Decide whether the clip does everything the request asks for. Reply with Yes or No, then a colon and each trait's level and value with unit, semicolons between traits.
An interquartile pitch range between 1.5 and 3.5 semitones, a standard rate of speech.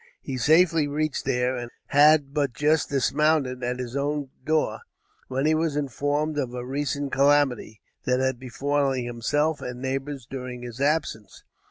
Yes: average, 2.7 semitones; average, 155 wpm